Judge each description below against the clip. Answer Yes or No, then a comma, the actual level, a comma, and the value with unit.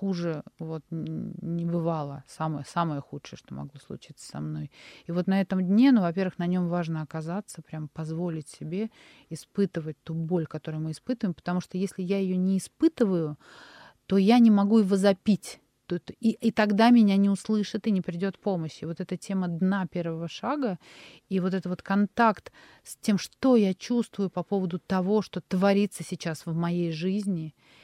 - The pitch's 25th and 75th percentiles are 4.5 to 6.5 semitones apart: No, average, 3.4 semitones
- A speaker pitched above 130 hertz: Yes, medium, 185 Hz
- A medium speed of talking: No, fast, 175 wpm